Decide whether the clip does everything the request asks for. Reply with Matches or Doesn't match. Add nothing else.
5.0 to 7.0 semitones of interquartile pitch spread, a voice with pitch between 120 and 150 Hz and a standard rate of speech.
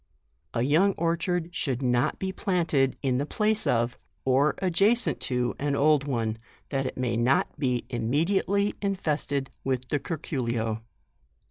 Matches